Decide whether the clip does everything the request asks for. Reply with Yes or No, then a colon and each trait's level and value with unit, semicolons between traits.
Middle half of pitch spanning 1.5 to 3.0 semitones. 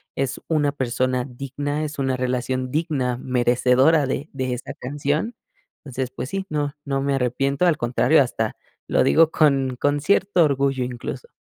Yes: narrow, 2.6 semitones